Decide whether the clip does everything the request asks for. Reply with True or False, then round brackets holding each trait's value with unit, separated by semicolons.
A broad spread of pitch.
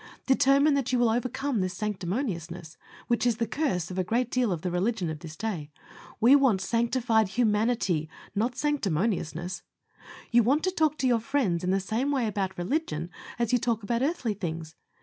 True (5.7 semitones)